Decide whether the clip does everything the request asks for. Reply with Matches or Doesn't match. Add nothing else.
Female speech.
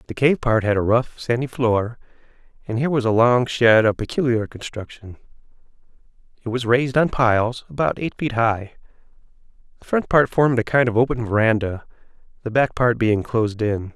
Doesn't match